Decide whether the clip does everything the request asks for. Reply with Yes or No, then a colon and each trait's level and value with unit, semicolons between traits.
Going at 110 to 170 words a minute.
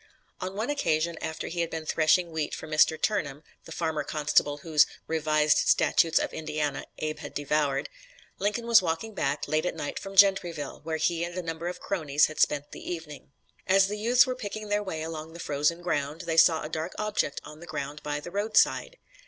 No: average, 200 wpm